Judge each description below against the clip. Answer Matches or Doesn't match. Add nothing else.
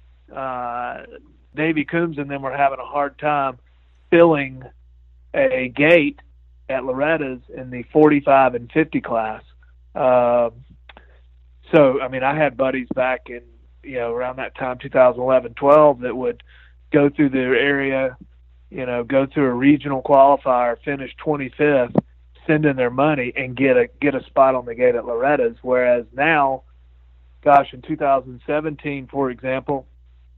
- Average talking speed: Matches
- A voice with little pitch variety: Doesn't match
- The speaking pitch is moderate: Doesn't match